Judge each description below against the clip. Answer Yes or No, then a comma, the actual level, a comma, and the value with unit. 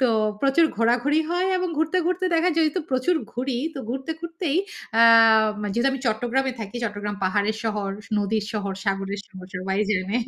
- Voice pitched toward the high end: Yes, high, 230 Hz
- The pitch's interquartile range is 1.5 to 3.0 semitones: No, average, 5.2 semitones